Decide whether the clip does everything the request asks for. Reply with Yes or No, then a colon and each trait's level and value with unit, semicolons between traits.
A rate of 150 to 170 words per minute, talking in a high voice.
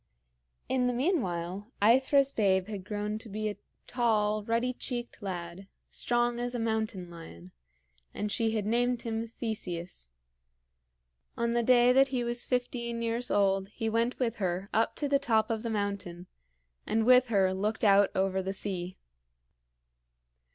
Yes: average, 155 wpm; high, 220 Hz